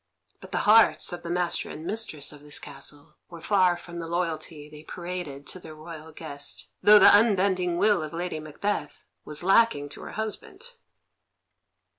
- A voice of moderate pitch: Yes, medium, 170 Hz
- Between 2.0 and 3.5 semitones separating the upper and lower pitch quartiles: No, average, 3.9 semitones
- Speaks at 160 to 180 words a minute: Yes, average, 170 wpm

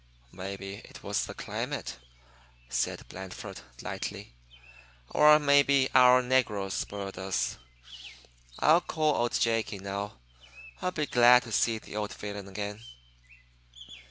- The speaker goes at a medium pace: No, slow, 125 wpm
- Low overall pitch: Yes, low, 110 Hz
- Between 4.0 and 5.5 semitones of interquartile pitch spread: Yes, average, 4.8 semitones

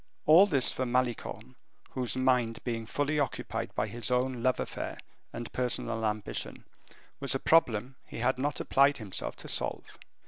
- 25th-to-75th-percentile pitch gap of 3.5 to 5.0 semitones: No, narrow, 2.5 semitones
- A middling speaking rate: Yes, average, 160 wpm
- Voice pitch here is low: Yes, low, 125 Hz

